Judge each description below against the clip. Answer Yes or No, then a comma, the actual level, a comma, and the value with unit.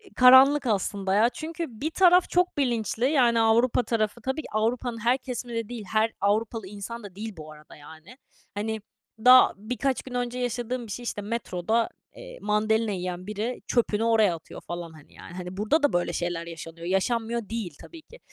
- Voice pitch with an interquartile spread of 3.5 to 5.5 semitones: Yes, average, 3.8 semitones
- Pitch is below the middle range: No, high, 225 Hz